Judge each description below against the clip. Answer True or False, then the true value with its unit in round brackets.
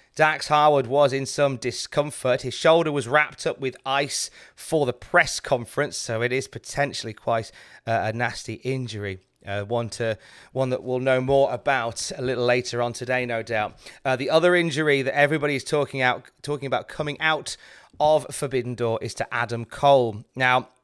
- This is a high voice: False (130 Hz)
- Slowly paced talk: False (180 wpm)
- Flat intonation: False (3.3 semitones)